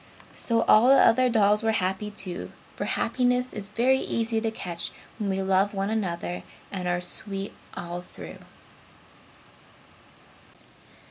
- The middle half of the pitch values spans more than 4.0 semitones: No, average, 3.4 semitones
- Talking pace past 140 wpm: No, slow, 135 wpm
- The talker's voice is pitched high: Yes, high, 205 Hz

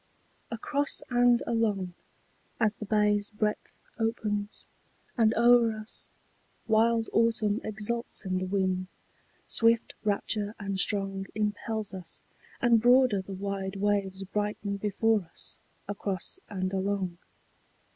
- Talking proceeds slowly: Yes, slow, 115 wpm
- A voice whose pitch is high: Yes, high, 210 Hz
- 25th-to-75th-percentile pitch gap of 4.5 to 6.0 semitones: No, narrow, 2.4 semitones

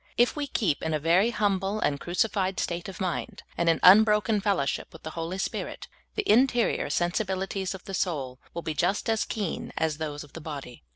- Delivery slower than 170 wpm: No, fast, 205 wpm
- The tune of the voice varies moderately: Yes, average, 4.6 semitones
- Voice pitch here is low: No, medium, 185 Hz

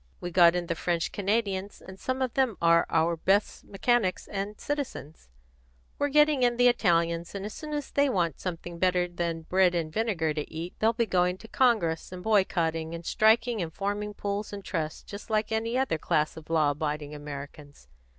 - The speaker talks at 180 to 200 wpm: Yes, average, 190 wpm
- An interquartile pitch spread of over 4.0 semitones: Yes, average, 4.9 semitones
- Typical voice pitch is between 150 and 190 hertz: Yes, medium, 185 Hz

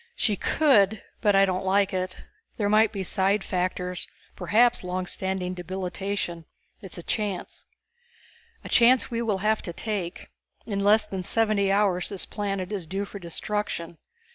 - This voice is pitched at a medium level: No, high, 195 Hz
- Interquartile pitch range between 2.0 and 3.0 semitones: Yes, narrow, 2.4 semitones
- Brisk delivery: No, average, 155 wpm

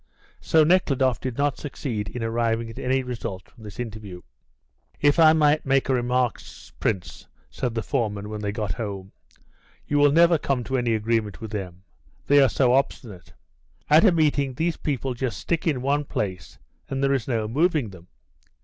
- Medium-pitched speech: No, low, 125 Hz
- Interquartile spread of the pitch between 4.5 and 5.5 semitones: Yes, average, 4.8 semitones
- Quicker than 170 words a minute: Yes, average, 180 wpm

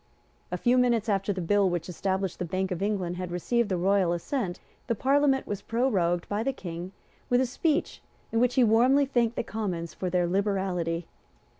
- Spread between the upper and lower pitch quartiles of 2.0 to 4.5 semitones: No, average, 5.0 semitones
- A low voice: No, high, 200 Hz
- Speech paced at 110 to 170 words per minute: No, average, 190 wpm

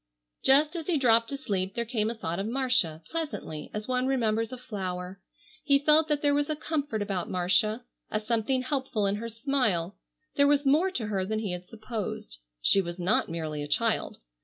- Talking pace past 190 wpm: Yes, average, 200 wpm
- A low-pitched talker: No, high, 225 Hz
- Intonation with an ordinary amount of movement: No, wide, 6.3 semitones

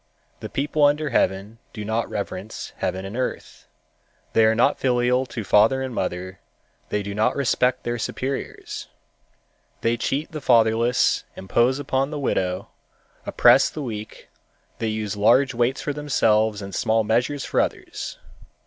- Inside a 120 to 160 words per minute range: Yes, average, 150 wpm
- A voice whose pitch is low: Yes, low, 115 Hz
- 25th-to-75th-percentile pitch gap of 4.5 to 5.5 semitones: No, average, 3.9 semitones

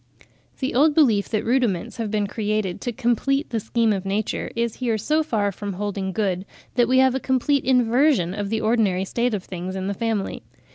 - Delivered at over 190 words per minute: Yes, average, 200 wpm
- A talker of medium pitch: No, high, 220 Hz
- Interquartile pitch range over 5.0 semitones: No, average, 3.7 semitones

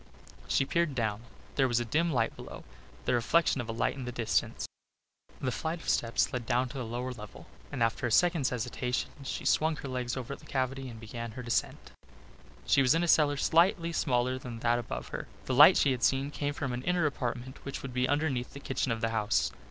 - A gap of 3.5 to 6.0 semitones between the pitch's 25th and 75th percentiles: No, average, 3.1 semitones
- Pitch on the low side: Yes, low, 130 Hz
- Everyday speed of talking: No, fast, 220 wpm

